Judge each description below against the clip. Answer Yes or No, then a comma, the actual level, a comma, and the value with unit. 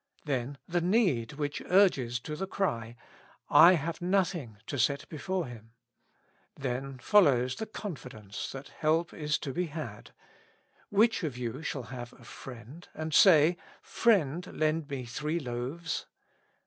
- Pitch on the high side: No, medium, 150 Hz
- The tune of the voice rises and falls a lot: Yes, wide, 5.7 semitones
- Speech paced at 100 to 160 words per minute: Yes, average, 150 wpm